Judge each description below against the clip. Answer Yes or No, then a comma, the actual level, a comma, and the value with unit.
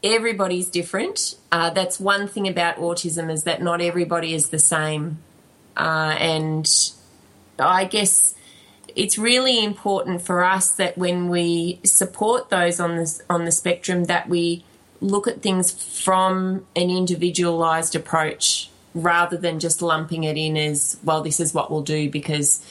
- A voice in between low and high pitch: Yes, medium, 175 Hz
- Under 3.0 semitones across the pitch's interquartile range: Yes, narrow, 2.6 semitones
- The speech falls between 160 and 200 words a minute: No, average, 150 wpm